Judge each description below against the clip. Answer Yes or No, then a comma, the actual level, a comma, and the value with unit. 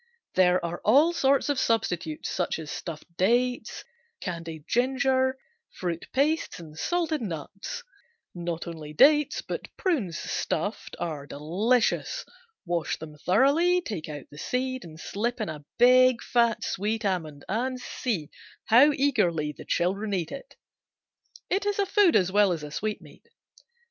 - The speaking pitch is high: Yes, high, 210 Hz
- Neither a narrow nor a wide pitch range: No, wide, 7.7 semitones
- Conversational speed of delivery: Yes, average, 145 wpm